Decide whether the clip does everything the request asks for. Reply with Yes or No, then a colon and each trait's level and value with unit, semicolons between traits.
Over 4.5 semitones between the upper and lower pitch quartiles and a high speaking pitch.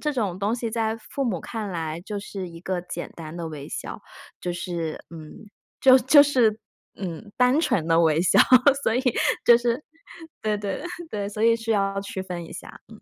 Yes: average, 4.9 semitones; high, 200 Hz